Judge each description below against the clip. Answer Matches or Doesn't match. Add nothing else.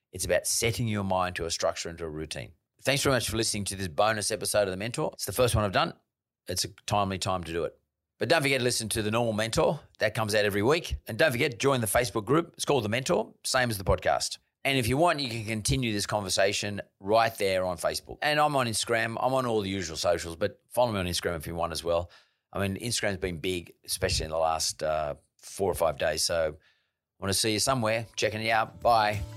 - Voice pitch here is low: Matches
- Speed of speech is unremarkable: Doesn't match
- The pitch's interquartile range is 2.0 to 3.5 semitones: Doesn't match